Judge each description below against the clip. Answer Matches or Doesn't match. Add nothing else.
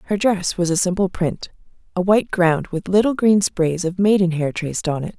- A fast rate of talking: Matches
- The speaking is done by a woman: Matches